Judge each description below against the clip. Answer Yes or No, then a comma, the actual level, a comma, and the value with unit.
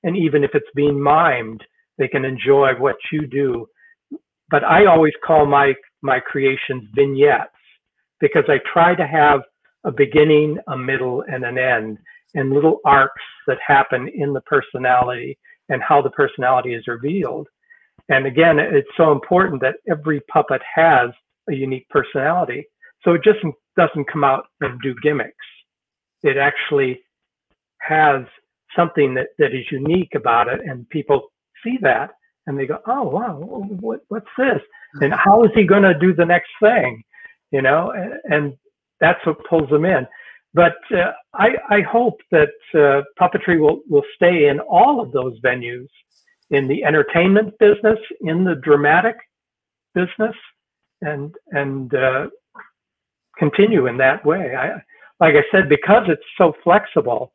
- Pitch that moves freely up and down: Yes, wide, 6.9 semitones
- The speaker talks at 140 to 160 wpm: Yes, average, 155 wpm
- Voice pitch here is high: No, medium, 155 Hz